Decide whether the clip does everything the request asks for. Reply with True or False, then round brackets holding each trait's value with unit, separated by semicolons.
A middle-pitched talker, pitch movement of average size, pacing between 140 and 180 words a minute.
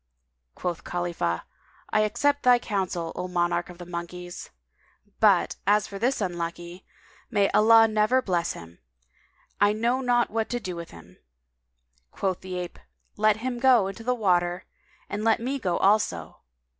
False (195 Hz; 4.4 semitones; 160 wpm)